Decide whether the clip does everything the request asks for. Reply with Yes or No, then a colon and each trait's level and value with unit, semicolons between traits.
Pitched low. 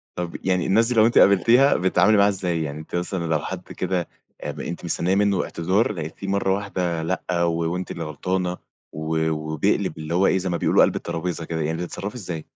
Yes: very low, 90 Hz